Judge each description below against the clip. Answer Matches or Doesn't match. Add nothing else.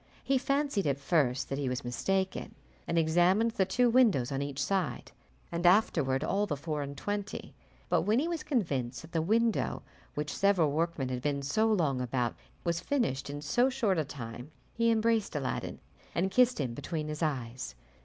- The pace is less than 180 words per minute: Doesn't match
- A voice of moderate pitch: Matches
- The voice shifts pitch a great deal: Matches